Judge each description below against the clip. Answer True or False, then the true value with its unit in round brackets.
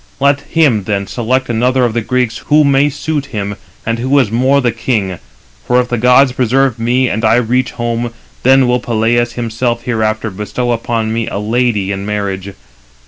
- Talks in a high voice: False (120 Hz)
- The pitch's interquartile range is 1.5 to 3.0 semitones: True (2.6 semitones)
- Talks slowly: False (185 wpm)